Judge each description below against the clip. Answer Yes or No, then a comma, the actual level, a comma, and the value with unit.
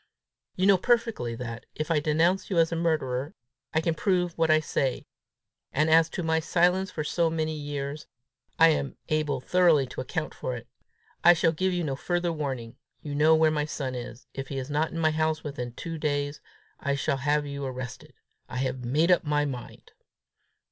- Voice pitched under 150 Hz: No, medium, 155 Hz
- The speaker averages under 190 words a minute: No, average, 195 wpm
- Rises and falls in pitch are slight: No, average, 3.2 semitones